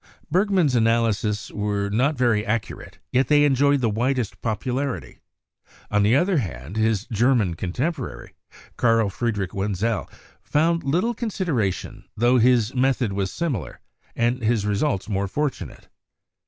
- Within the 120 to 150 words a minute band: Yes, average, 140 wpm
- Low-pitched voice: Yes, low, 115 Hz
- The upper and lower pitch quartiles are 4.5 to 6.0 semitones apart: Yes, average, 4.8 semitones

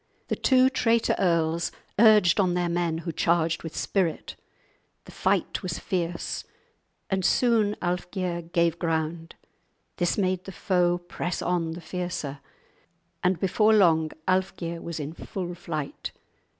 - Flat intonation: Yes, narrow, 2.1 semitones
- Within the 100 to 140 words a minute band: Yes, slow, 135 wpm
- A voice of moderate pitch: Yes, medium, 175 Hz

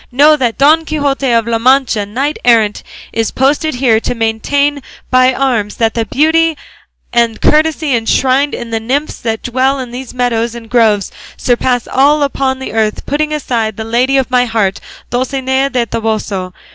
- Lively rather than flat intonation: No, average, 3.4 semitones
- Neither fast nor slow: Yes, average, 165 wpm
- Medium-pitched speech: No, very high, 250 Hz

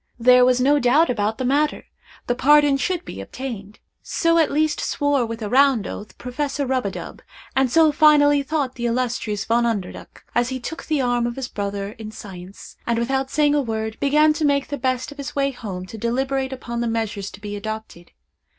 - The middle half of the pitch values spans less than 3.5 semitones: No, average, 4.1 semitones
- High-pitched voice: Yes, very high, 250 Hz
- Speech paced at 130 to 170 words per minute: No, fast, 205 wpm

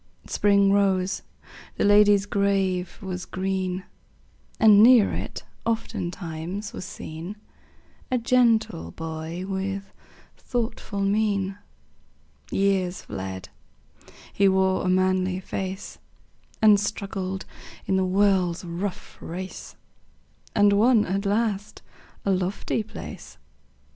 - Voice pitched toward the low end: No, high, 195 Hz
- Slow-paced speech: Yes, slow, 100 wpm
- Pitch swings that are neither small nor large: No, narrow, 1.8 semitones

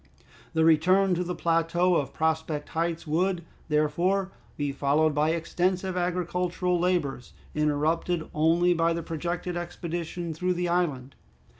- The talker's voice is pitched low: No, medium, 170 Hz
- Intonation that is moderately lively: No, narrow, 2.2 semitones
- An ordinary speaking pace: No, slow, 130 wpm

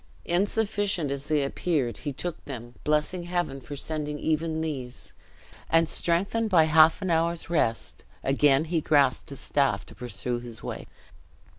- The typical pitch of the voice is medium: Yes, medium, 155 Hz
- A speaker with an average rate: Yes, average, 150 wpm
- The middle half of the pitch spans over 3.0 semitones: Yes, average, 3.7 semitones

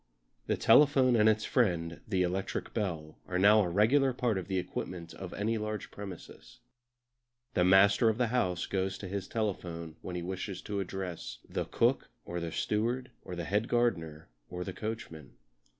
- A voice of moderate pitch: No, very low, 95 Hz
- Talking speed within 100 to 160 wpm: No, average, 175 wpm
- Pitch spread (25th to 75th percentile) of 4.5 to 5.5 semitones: No, average, 3.6 semitones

